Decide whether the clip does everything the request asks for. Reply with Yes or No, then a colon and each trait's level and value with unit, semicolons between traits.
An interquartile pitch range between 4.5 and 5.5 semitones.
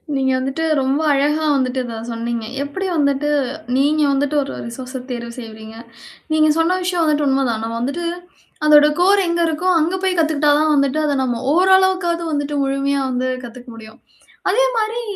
No: average, 3.9 semitones